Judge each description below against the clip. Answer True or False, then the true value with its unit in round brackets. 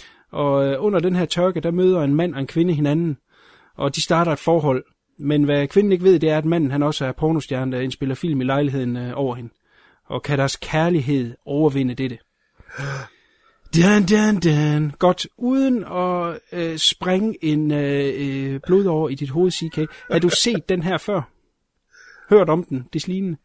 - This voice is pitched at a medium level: True (155 Hz)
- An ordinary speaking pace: True (180 wpm)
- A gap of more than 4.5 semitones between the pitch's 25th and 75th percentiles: False (4.2 semitones)